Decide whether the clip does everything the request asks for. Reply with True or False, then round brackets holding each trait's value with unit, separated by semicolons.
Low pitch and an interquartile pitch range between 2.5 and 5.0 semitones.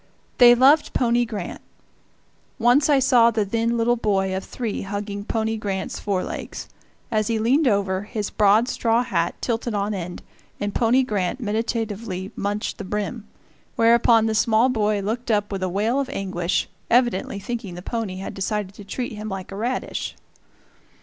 False (215 Hz; 2.9 semitones)